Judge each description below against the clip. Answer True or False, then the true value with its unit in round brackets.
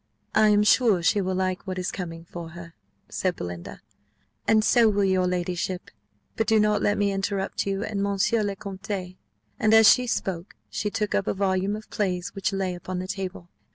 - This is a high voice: True (195 Hz)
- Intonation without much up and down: True (2.3 semitones)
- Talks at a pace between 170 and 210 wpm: True (195 wpm)